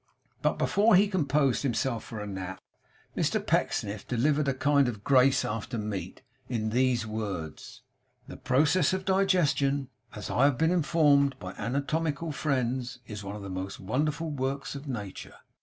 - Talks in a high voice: No, low, 130 Hz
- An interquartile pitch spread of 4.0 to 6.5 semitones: Yes, average, 5.3 semitones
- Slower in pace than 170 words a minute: Yes, average, 155 wpm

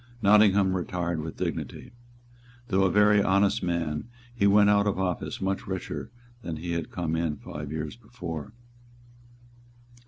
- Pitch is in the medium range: No, very low, 95 Hz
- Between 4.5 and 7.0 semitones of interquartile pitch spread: No, average, 3.5 semitones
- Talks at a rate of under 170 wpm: Yes, average, 145 wpm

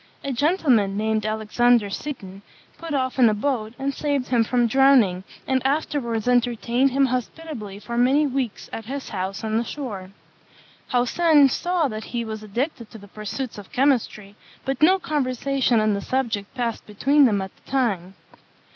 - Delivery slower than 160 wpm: No, average, 165 wpm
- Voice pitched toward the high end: Yes, high, 245 Hz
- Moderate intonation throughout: Yes, average, 4.1 semitones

